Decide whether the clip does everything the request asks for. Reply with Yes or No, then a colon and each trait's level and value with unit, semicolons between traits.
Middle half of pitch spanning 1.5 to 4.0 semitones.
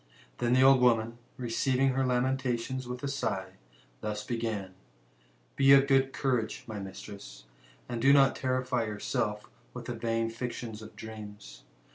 Yes: average, 3.5 semitones